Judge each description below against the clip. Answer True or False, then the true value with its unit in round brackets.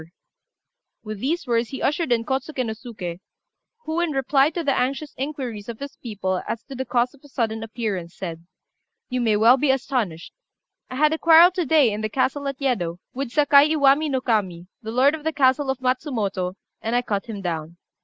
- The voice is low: False (255 Hz)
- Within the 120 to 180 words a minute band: False (205 wpm)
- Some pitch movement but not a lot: True (4.6 semitones)